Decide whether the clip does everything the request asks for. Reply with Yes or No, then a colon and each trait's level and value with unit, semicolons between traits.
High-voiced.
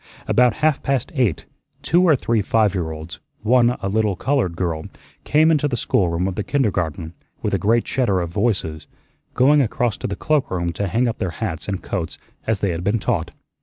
No: low, 105 Hz